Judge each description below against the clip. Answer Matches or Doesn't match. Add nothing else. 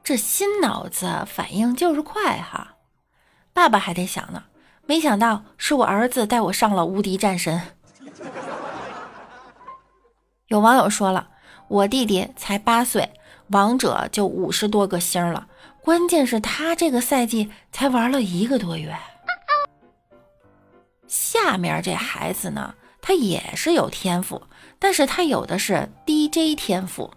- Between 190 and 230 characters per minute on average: Matches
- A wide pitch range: Matches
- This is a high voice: Matches